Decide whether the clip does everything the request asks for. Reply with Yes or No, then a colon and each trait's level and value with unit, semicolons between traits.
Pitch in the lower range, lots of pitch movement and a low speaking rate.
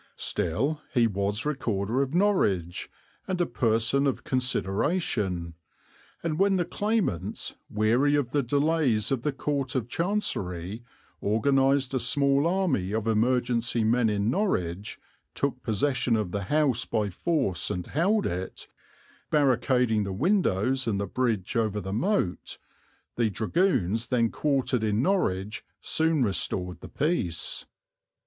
Yes: low, 125 Hz; wide, 6.0 semitones; slow, 130 wpm